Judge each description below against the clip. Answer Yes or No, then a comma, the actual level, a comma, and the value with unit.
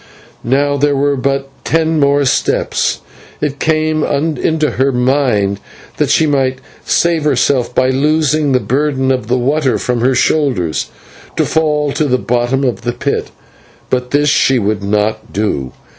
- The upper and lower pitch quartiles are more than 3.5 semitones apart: No, average, 3.1 semitones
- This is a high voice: No, low, 135 Hz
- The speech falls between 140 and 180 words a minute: Yes, average, 150 wpm